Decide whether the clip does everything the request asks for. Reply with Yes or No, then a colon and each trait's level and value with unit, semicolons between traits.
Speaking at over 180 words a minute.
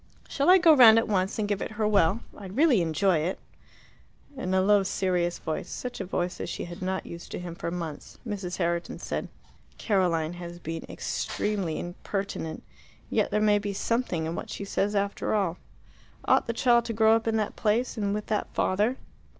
Yes: average, 200 wpm